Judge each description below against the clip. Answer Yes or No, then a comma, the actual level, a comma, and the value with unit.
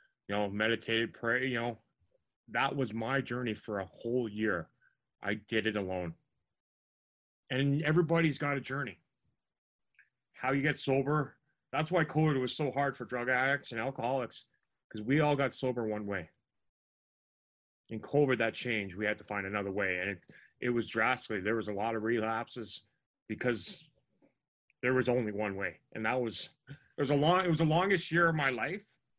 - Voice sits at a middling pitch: No, low, 120 Hz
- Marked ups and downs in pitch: No, average, 4.6 semitones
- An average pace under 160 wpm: No, average, 180 wpm